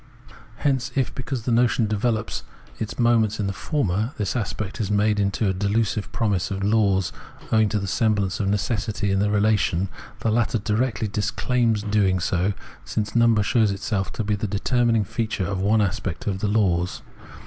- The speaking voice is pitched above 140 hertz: No, low, 105 Hz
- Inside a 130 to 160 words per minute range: No, average, 170 wpm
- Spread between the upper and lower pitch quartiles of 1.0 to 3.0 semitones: Yes, narrow, 2.4 semitones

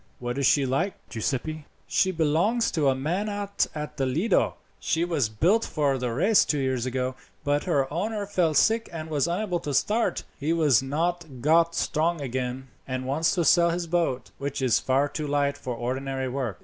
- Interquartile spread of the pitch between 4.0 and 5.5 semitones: Yes, average, 4.5 semitones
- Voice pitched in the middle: Yes, medium, 150 Hz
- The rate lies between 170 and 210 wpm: Yes, average, 190 wpm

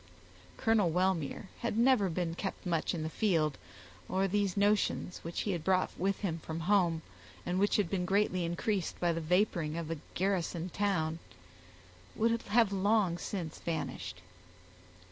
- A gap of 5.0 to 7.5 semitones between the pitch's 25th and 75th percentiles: No, average, 3.4 semitones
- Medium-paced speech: Yes, average, 155 wpm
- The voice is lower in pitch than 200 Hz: Yes, medium, 185 Hz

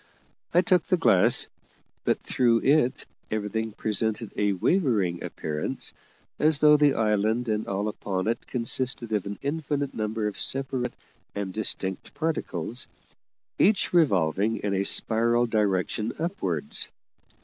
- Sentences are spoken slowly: Yes, slow, 125 wpm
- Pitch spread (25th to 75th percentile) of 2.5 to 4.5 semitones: No, average, 5.1 semitones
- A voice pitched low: Yes, low, 110 Hz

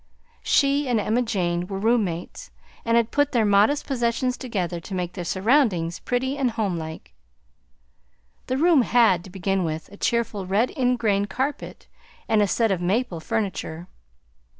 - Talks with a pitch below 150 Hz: No, high, 215 Hz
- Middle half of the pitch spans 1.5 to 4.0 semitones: No, average, 5.2 semitones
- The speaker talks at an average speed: Yes, average, 155 wpm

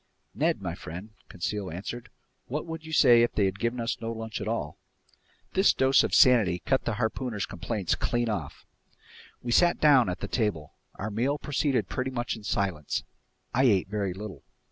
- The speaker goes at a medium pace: Yes, average, 180 wpm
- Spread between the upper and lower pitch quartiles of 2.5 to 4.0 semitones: No, average, 4.5 semitones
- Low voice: Yes, low, 115 Hz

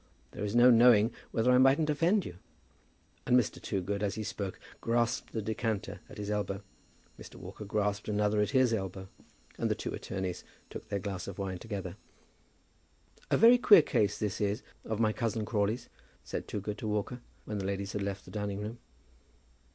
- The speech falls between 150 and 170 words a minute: No, average, 180 wpm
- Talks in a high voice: No, low, 105 Hz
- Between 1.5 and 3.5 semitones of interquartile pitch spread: Yes, average, 2.7 semitones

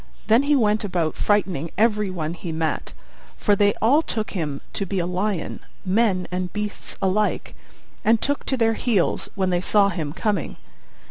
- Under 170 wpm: No, average, 175 wpm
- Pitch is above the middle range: Yes, high, 200 Hz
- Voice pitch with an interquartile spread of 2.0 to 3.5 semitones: Yes, average, 3.2 semitones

